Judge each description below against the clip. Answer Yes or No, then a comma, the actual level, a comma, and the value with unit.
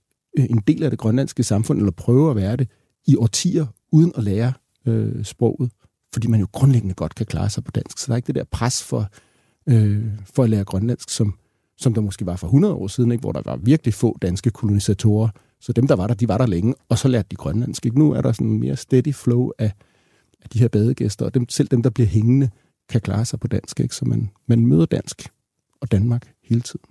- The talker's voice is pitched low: Yes, low, 120 Hz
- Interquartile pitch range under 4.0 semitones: Yes, average, 3.5 semitones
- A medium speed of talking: No, fast, 240 wpm